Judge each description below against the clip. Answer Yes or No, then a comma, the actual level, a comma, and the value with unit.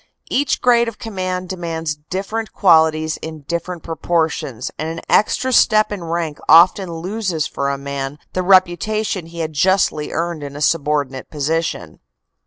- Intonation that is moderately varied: Yes, average, 3.5 semitones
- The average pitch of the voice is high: No, medium, 165 Hz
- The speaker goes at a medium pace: Yes, average, 155 wpm